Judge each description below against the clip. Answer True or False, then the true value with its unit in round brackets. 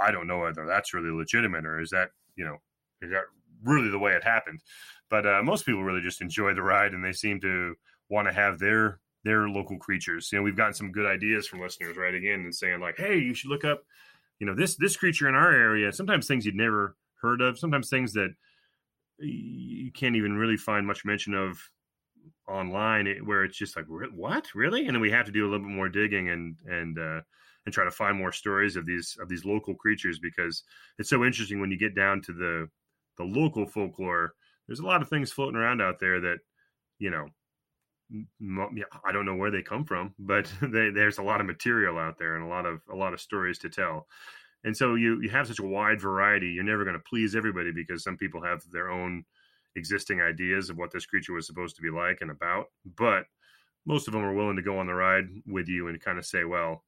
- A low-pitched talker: True (100 Hz)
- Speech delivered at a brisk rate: True (230 wpm)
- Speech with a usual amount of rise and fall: True (3.3 semitones)